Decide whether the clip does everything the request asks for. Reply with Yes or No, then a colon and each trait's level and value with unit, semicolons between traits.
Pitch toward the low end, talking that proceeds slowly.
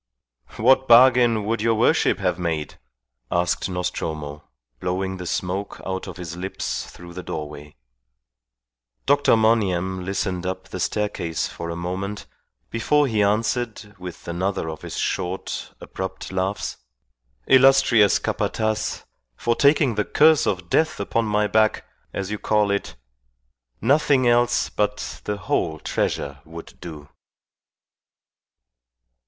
Yes: low, 100 Hz; slow, 125 wpm